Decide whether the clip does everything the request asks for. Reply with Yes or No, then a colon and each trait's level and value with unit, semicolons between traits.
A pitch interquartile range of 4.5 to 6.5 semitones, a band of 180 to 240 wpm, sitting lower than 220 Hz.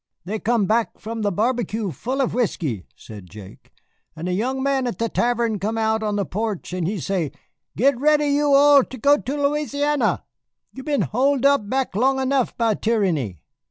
No: average, 5.1 semitones; average, 185 wpm; high, 230 Hz